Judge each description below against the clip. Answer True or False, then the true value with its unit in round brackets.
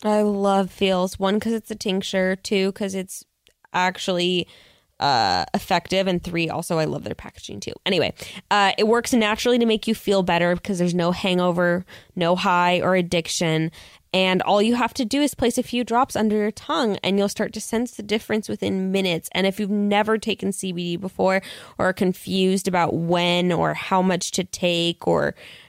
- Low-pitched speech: False (190 Hz)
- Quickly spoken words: False (190 wpm)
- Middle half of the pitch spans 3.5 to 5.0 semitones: False (2.9 semitones)